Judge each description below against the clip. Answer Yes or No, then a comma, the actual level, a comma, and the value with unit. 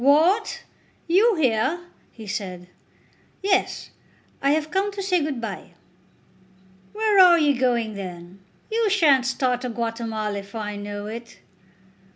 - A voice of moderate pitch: No, very high, 250 Hz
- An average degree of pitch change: No, wide, 8.6 semitones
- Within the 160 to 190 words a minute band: No, slow, 135 wpm